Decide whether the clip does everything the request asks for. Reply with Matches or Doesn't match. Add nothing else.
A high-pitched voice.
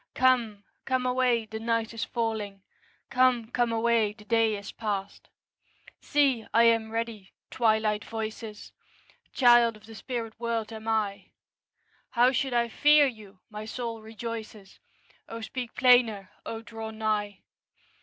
Matches